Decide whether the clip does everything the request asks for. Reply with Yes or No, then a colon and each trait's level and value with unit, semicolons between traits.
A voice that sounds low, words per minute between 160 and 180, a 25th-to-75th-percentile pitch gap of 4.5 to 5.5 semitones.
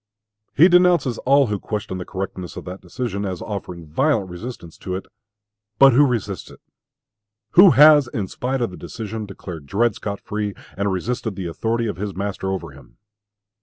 Yes: low, 105 Hz; average, 175 wpm; average, 4.9 semitones